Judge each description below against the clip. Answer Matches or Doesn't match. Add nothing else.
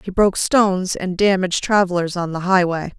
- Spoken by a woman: Matches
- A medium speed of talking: Matches